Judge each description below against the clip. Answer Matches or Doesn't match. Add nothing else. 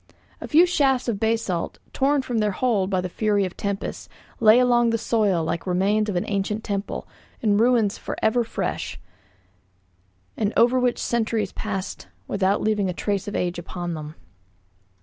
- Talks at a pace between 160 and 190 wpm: Matches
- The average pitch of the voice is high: Matches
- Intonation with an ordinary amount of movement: Matches